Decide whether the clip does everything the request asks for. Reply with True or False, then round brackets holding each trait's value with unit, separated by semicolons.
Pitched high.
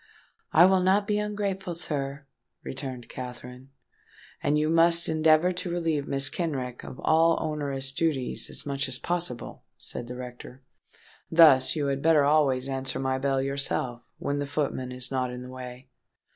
False (140 Hz)